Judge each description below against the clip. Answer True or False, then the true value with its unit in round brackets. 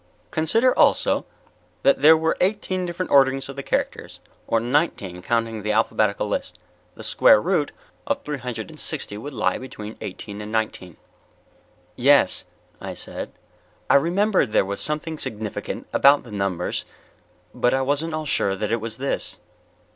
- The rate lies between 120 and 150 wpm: False (160 wpm)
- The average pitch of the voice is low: True (130 Hz)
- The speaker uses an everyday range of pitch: False (7.0 semitones)